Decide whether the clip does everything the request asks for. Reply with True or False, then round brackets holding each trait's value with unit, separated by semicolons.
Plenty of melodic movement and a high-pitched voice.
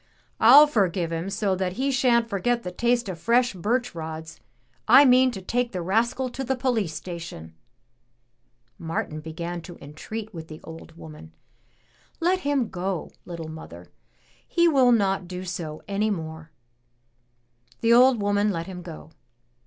True (6.4 semitones; 195 Hz)